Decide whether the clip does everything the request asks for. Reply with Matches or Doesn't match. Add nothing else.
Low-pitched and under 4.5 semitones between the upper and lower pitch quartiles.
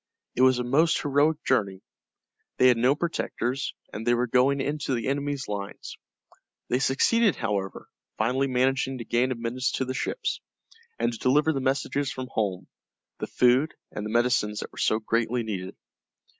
Matches